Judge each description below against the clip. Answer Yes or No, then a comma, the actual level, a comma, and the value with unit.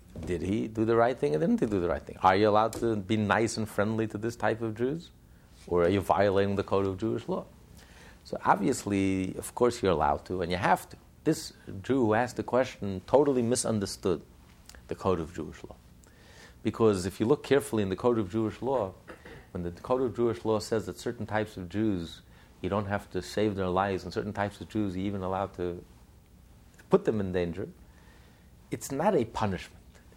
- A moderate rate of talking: No, fast, 210 wpm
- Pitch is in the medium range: No, low, 100 Hz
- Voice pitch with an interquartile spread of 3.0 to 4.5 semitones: Yes, average, 3.7 semitones